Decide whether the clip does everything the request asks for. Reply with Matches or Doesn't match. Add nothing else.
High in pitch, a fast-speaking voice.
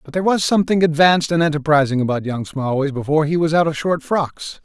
Doesn't match